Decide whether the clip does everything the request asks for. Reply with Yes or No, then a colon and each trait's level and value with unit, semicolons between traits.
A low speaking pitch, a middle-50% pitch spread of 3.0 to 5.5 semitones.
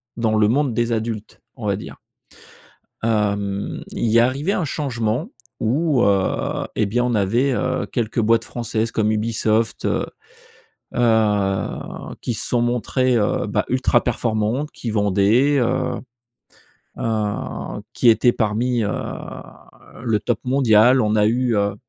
No: low, 115 Hz; narrow, 2.5 semitones